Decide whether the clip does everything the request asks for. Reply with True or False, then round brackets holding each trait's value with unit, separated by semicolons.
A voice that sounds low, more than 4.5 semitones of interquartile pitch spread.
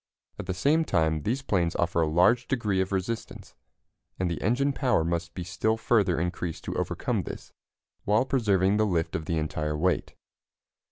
True (95 Hz; 4.9 semitones)